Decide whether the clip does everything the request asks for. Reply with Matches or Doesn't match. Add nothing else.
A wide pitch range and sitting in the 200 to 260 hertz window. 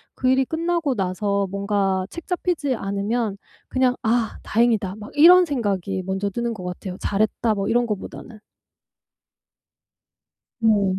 Doesn't match